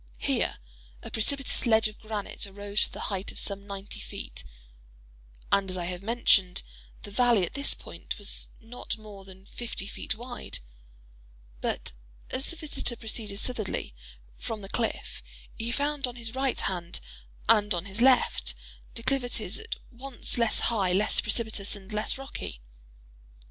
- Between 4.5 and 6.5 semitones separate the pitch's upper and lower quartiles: No, average, 3.6 semitones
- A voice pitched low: No, high, 215 Hz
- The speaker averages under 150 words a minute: No, average, 155 wpm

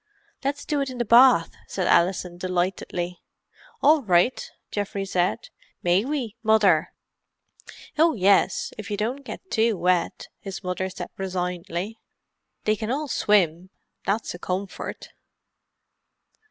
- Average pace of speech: No, slow, 125 wpm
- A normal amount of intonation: Yes, average, 4.6 semitones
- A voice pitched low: No, high, 195 Hz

